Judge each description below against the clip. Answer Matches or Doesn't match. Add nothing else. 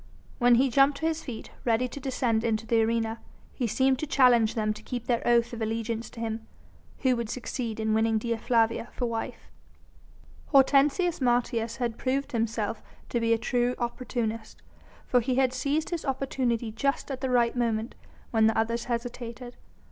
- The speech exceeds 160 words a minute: Matches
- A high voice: Matches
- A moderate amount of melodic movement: Doesn't match